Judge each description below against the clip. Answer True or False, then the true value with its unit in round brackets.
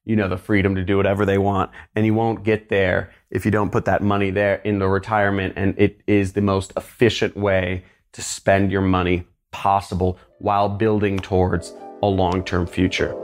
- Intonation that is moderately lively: False (1.6 semitones)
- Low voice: True (100 Hz)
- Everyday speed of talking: True (195 wpm)